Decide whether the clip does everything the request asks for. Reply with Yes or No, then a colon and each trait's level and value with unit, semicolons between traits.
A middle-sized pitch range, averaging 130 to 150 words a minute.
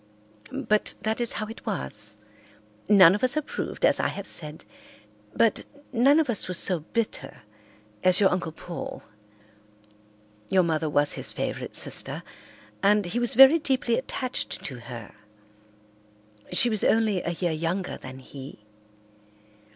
No: wide, 6.6 semitones; average, 145 wpm